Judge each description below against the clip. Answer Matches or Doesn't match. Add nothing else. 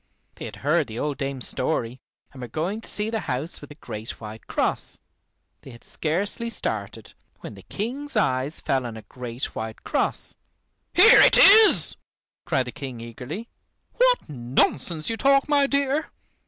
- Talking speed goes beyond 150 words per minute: Matches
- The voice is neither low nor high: Matches